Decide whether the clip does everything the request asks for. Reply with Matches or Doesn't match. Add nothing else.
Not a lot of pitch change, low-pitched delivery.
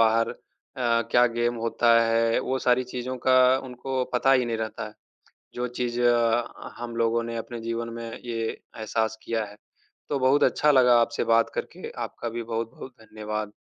Matches